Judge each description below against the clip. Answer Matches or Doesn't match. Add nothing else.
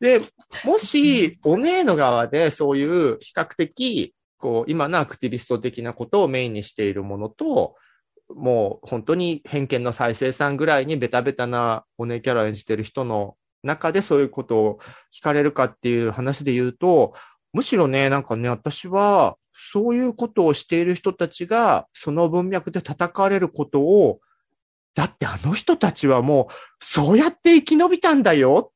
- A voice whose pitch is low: Doesn't match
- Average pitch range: Doesn't match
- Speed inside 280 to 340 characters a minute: Matches